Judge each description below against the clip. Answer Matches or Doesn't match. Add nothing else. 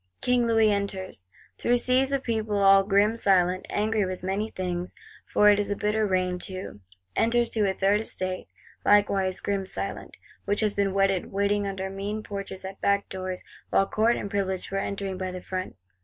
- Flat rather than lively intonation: Matches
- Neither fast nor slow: Matches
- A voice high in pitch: Matches